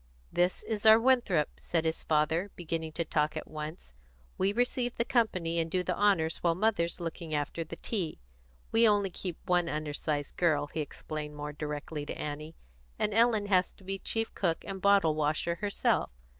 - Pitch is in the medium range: Yes, medium, 170 Hz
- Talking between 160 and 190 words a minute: Yes, average, 175 wpm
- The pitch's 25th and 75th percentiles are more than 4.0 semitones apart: Yes, average, 4.7 semitones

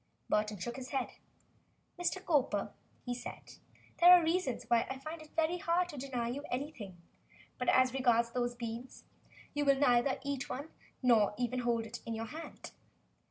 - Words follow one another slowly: No, average, 175 wpm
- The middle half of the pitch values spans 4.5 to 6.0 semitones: No, average, 3.7 semitones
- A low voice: No, very high, 255 Hz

